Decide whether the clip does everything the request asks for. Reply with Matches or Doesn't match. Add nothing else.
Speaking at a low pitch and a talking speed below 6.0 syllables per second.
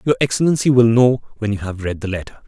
Doesn't match